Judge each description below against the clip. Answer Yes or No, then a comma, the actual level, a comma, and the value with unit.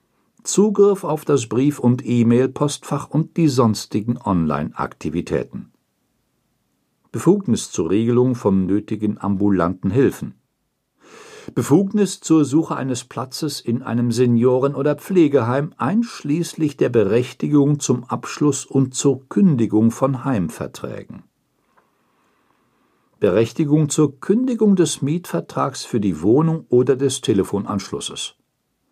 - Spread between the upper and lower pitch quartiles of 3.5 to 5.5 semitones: Yes, average, 4.7 semitones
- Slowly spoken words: Yes, slow, 100 wpm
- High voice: No, low, 135 Hz